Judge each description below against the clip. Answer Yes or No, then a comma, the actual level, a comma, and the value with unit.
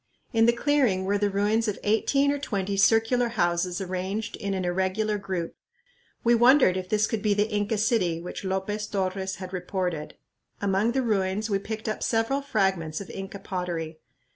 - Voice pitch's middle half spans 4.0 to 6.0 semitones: No, average, 3.0 semitones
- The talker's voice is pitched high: Yes, high, 200 Hz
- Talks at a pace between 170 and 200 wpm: Yes, average, 175 wpm